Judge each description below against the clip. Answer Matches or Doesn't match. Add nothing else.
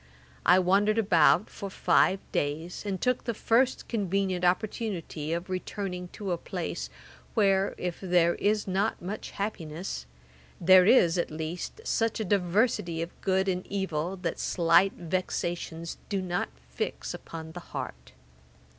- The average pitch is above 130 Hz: Matches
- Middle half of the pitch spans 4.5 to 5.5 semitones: Doesn't match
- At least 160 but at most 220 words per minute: Doesn't match